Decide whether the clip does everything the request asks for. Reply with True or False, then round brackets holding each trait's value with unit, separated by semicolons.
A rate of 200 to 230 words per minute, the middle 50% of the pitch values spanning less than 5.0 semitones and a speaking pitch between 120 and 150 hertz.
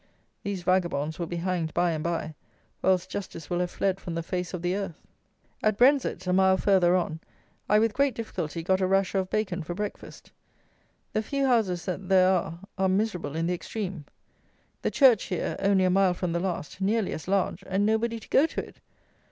False (205 wpm; 2.6 semitones; 185 Hz)